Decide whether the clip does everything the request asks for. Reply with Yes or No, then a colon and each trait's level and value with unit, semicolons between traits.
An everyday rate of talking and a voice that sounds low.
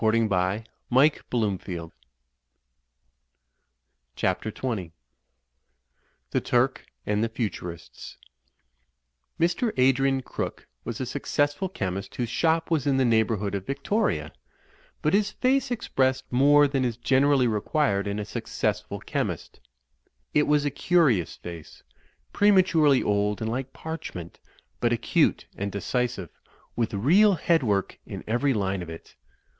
No: slow, 125 wpm; low, 125 Hz